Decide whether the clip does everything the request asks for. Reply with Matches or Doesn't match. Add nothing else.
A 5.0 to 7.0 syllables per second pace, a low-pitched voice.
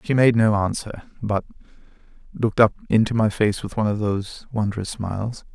Matches